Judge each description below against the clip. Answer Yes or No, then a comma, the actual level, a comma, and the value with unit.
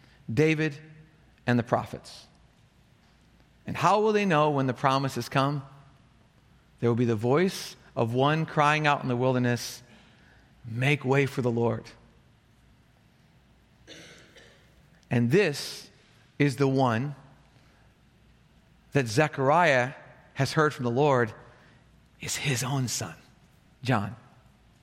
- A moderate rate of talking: No, slow, 115 wpm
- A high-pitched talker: No, low, 135 Hz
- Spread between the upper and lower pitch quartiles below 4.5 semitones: Yes, average, 3.4 semitones